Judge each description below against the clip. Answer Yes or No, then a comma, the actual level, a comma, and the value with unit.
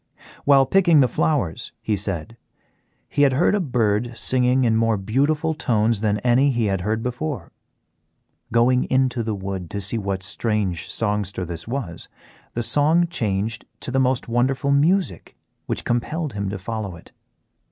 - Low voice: Yes, low, 120 Hz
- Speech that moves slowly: No, average, 155 wpm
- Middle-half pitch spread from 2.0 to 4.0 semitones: No, average, 4.8 semitones